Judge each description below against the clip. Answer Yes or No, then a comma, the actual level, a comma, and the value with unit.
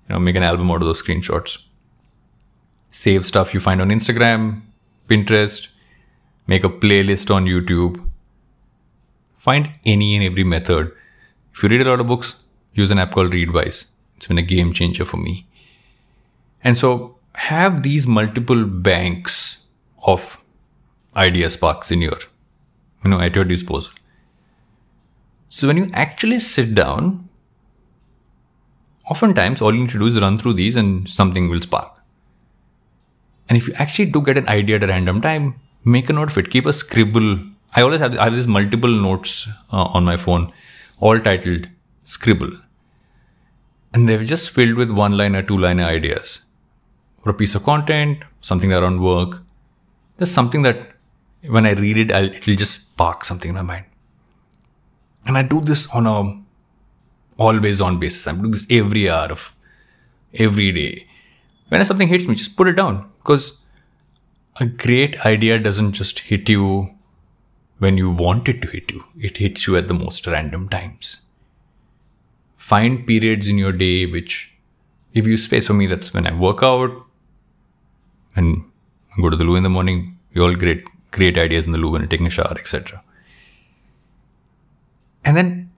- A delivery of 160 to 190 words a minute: Yes, average, 165 wpm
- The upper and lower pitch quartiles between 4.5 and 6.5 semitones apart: Yes, average, 5.0 semitones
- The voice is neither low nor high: No, low, 105 Hz